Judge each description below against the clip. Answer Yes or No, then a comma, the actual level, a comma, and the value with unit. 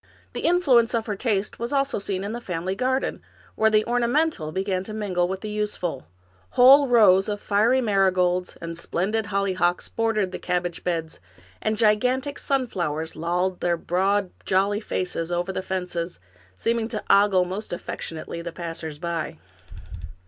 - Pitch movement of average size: Yes, average, 4.1 semitones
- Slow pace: No, average, 155 wpm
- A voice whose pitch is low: No, high, 195 Hz